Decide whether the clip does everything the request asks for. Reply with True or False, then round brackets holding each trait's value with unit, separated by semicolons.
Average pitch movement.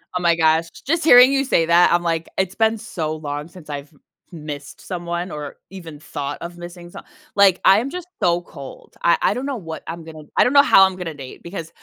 True (3.4 semitones)